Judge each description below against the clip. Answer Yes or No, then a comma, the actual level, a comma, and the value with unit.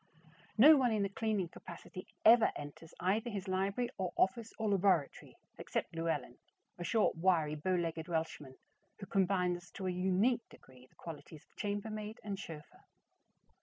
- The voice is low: No, medium, 185 Hz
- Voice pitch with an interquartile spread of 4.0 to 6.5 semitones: Yes, average, 4.3 semitones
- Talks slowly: No, average, 155 wpm